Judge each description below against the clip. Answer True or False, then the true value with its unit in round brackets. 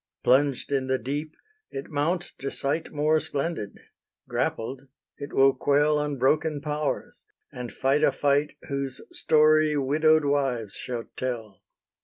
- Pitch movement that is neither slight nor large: False (2.3 semitones)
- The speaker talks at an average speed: False (130 wpm)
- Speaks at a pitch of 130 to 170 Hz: True (140 Hz)